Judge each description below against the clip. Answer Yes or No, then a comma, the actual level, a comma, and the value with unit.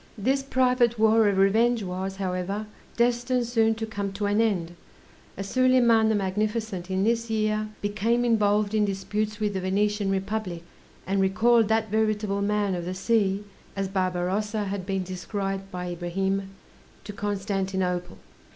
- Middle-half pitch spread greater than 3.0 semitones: No, narrow, 2.4 semitones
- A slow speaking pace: No, average, 150 wpm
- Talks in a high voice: Yes, high, 205 Hz